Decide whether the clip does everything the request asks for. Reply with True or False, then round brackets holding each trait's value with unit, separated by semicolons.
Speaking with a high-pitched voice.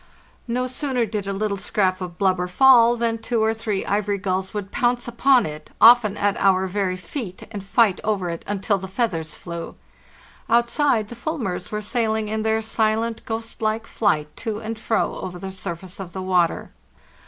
True (210 Hz)